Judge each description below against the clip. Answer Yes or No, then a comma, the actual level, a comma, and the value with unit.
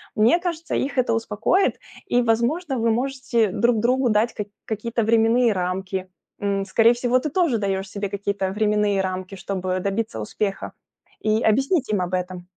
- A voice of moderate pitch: No, high, 220 Hz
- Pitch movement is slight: No, average, 3.8 semitones